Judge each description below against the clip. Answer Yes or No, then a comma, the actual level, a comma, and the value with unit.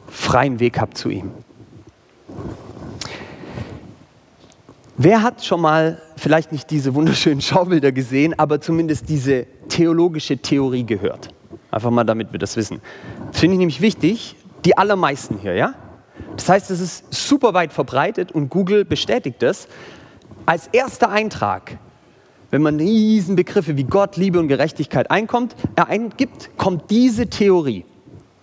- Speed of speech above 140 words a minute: No, average, 135 wpm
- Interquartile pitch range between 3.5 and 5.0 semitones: No, wide, 5.5 semitones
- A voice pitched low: No, medium, 160 Hz